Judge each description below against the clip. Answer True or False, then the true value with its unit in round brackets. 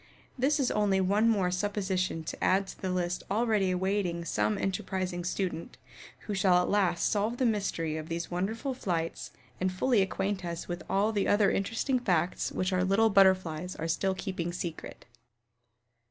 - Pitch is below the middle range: False (190 Hz)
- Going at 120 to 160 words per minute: False (170 wpm)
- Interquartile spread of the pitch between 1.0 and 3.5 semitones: True (2.6 semitones)